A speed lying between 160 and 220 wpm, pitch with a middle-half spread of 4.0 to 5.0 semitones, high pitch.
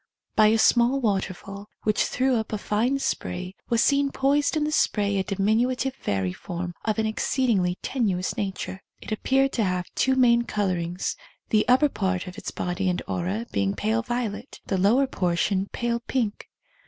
Yes: average, 170 wpm; average, 4.7 semitones; high, 215 Hz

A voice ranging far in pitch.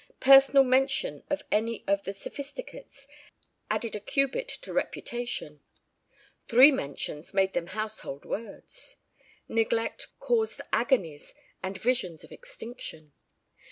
Yes: wide, 6.2 semitones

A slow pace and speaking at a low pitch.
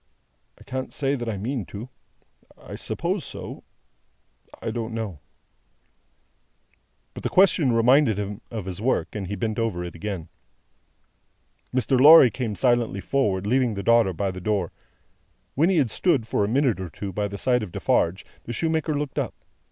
No: average, 170 wpm; low, 115 Hz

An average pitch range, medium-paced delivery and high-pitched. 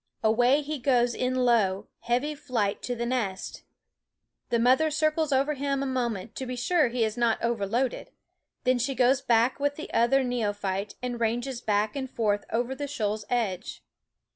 Yes: average, 3.1 semitones; average, 170 wpm; high, 245 Hz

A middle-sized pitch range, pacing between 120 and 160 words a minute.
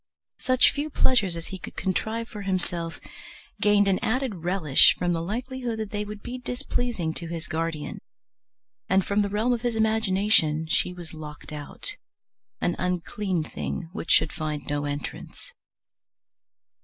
Yes: average, 5.0 semitones; average, 155 wpm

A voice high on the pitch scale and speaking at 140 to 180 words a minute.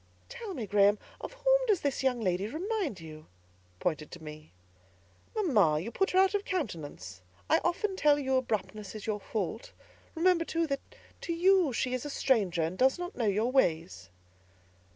Yes: very high, 250 Hz; average, 175 wpm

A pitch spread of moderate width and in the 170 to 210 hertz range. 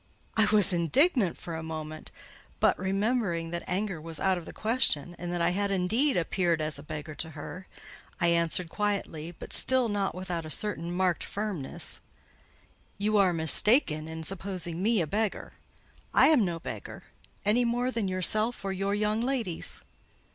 Yes: average, 4.2 semitones; medium, 185 Hz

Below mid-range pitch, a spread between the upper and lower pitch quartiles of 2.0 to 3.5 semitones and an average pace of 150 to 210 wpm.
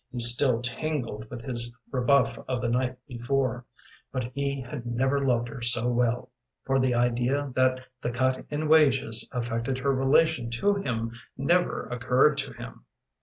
Yes: low, 125 Hz; narrow, 2.4 semitones; average, 160 wpm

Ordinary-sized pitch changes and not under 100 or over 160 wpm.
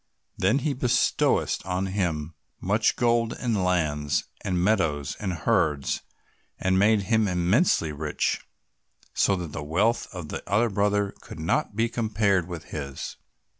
Yes: average, 5.0 semitones; average, 140 wpm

